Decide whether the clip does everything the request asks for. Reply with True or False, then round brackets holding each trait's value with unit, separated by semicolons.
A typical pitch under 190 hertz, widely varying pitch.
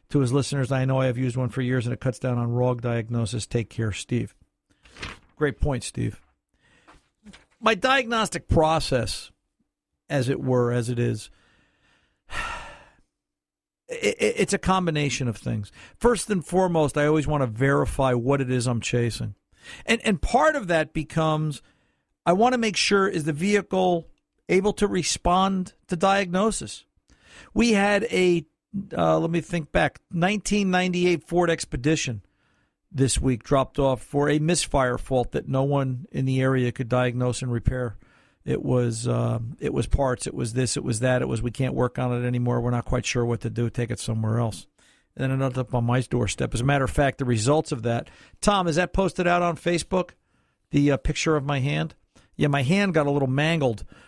True (140 Hz; 6.3 semitones)